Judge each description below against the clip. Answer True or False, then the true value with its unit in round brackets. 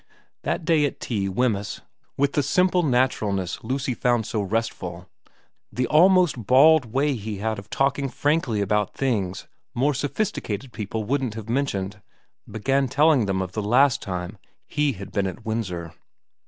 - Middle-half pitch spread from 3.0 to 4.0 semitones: False (5.4 semitones)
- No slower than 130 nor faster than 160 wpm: True (155 wpm)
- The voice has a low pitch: True (115 Hz)